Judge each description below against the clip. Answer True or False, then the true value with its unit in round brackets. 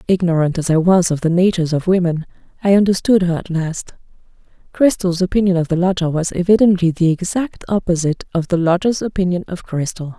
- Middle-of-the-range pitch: True (180 Hz)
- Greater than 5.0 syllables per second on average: True (5.9 syllables/s)